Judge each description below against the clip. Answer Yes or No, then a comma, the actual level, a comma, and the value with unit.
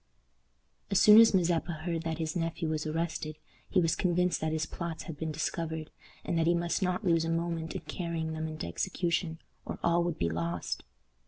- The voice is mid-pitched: Yes, medium, 165 Hz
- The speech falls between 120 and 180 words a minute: No, average, 195 wpm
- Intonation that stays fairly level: Yes, narrow, 1.6 semitones